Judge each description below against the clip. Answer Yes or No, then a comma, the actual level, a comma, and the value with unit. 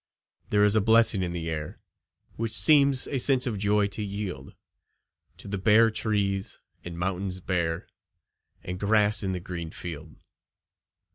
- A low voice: Yes, low, 100 Hz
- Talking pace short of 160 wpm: Yes, average, 150 wpm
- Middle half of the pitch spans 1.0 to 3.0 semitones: No, average, 3.5 semitones